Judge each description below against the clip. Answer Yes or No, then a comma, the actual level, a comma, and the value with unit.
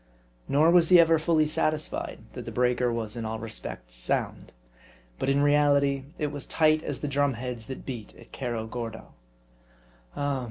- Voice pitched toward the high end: No, low, 135 Hz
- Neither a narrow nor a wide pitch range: Yes, average, 4.2 semitones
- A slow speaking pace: No, average, 170 wpm